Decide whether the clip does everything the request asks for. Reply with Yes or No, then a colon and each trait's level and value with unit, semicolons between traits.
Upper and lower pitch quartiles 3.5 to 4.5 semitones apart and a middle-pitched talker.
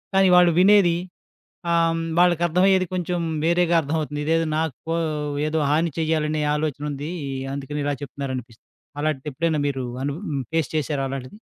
No: average, 3.0 semitones; medium, 155 Hz